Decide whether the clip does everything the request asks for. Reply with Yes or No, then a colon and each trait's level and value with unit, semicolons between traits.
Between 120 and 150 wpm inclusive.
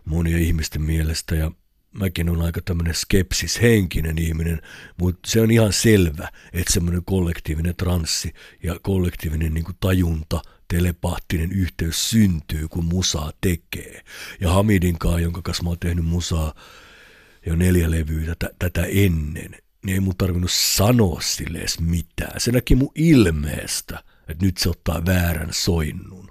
Yes: average, 145 wpm